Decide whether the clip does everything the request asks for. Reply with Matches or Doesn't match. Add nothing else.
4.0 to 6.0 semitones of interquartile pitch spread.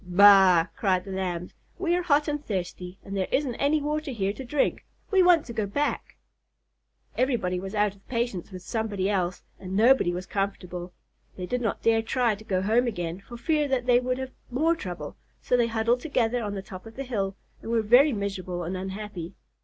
Matches